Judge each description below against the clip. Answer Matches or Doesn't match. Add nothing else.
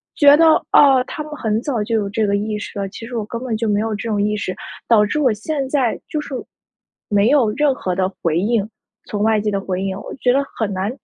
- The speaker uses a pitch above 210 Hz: Matches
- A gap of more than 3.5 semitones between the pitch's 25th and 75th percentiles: Matches